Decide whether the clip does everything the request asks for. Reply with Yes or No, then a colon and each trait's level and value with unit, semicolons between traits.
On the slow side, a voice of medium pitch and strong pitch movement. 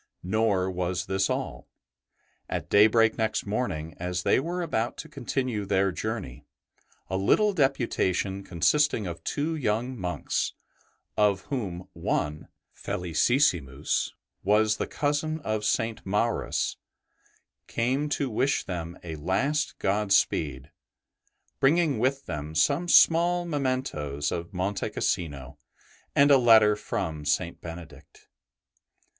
No: slow, 115 wpm; low, 105 Hz; wide, 7.1 semitones